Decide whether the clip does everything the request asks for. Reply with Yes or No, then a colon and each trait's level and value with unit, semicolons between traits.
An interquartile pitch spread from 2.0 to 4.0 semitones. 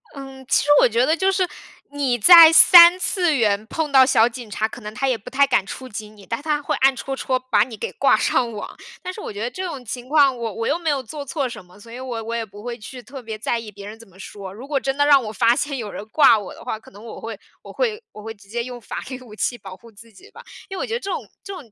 No: average, 4.6 semitones